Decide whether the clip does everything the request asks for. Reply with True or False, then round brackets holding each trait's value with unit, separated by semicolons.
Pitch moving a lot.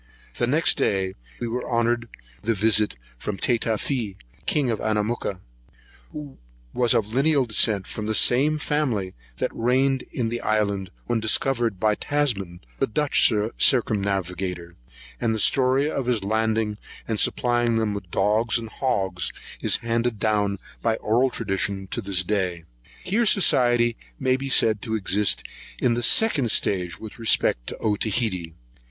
False (3.3 semitones)